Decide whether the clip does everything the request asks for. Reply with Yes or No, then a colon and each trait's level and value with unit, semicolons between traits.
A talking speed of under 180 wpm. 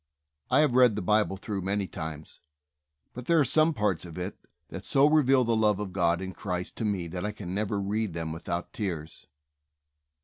No: average, 200 wpm